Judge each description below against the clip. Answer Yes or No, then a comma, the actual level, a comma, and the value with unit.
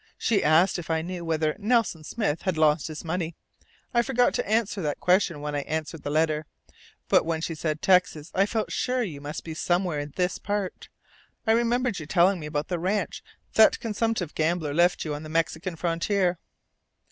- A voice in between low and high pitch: Yes, medium, 170 Hz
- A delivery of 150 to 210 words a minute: Yes, average, 195 wpm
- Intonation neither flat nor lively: Yes, average, 4.1 semitones